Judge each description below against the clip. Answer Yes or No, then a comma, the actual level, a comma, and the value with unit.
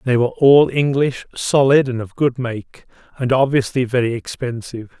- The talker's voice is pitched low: Yes, low, 125 Hz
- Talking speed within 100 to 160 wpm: Yes, average, 155 wpm